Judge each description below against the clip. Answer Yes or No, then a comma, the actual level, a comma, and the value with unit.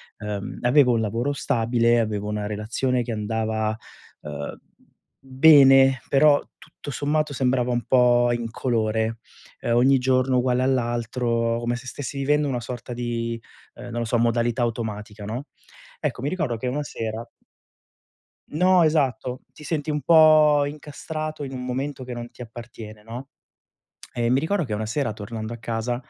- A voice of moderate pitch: No, low, 120 Hz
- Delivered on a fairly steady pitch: No, average, 3.0 semitones